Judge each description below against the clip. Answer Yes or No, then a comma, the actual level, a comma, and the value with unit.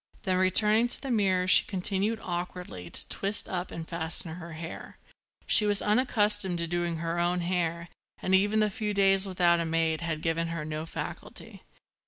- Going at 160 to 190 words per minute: Yes, average, 180 wpm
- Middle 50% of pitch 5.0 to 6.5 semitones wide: No, average, 3.1 semitones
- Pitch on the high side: No, medium, 180 Hz